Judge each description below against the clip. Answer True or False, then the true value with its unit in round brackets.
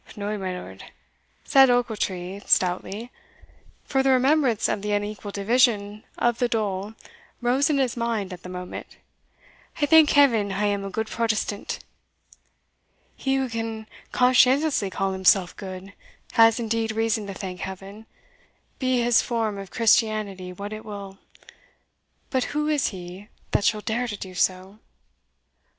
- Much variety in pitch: False (3.7 semitones)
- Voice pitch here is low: False (215 Hz)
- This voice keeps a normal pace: True (145 wpm)